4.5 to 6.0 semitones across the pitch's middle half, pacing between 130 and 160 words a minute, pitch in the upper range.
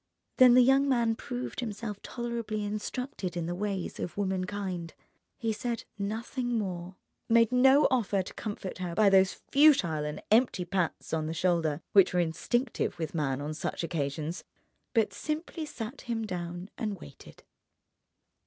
Yes: average, 5.3 semitones; average, 155 wpm; high, 205 Hz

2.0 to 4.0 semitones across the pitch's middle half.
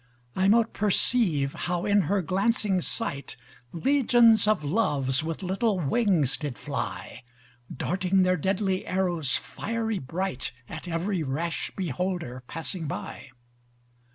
No: average, 4.5 semitones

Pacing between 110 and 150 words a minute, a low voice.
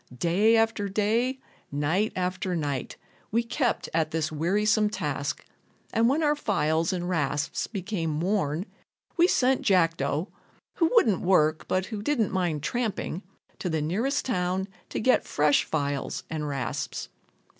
No: average, 140 wpm; medium, 185 Hz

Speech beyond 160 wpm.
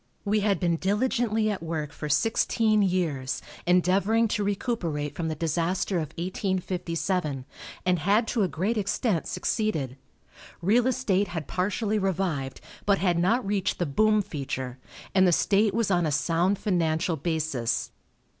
No: average, 145 wpm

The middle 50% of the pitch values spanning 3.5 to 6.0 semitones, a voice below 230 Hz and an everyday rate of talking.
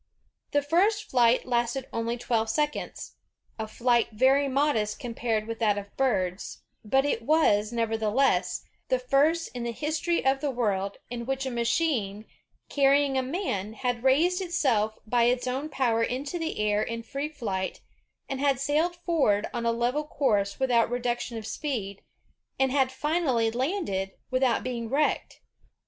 No: average, 4.1 semitones; very high, 250 Hz; average, 155 wpm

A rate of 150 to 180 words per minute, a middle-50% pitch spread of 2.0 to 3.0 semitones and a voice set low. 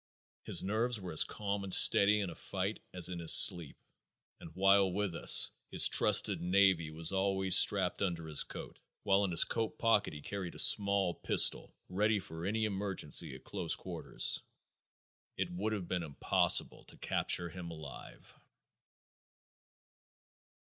Yes: average, 155 wpm; average, 2.7 semitones; very low, 95 Hz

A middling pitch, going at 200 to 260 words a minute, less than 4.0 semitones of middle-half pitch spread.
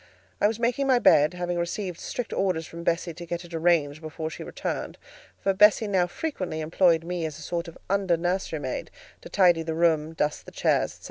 Yes: medium, 170 Hz; fast, 205 wpm; average, 2.9 semitones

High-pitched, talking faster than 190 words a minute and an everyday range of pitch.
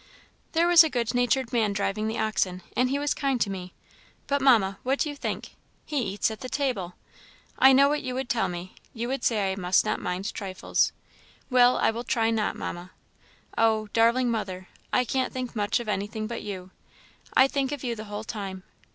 Yes: high, 225 Hz; fast, 205 wpm; average, 4.4 semitones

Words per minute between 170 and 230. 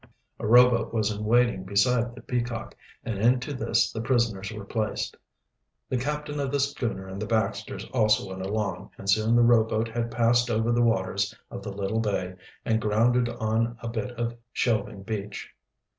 Yes: average, 175 wpm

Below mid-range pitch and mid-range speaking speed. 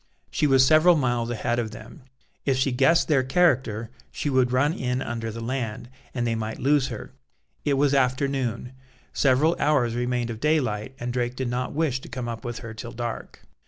Yes: low, 125 Hz; average, 195 wpm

